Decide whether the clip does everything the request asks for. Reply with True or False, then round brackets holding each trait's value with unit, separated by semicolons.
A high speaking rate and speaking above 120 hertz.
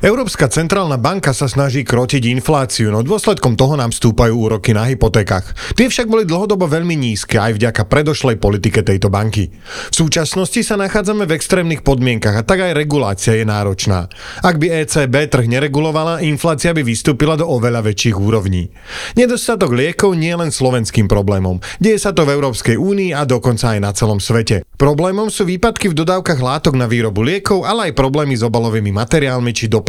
True (175 wpm; 135 Hz)